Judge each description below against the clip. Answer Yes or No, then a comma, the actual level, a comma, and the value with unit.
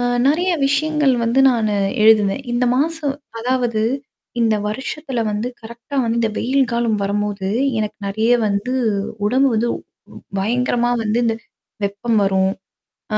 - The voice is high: Yes, high, 235 Hz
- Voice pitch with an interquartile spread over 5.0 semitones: No, average, 3.8 semitones